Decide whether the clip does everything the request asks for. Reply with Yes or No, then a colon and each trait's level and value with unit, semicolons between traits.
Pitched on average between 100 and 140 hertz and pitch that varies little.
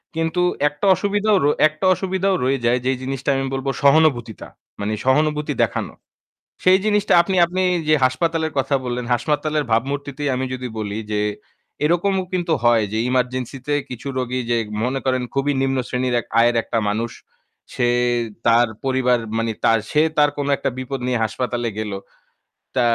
No: low, 135 Hz; average, 4.2 semitones